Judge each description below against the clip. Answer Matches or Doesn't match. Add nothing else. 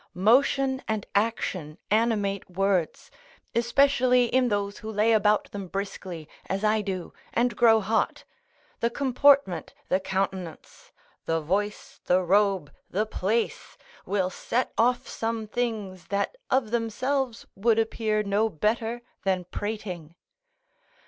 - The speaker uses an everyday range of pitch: Matches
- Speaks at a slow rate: Matches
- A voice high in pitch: Matches